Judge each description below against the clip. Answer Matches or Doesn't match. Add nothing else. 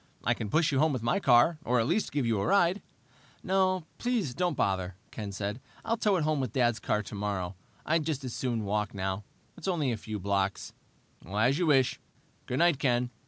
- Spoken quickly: Matches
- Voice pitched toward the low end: Matches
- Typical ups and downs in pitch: Doesn't match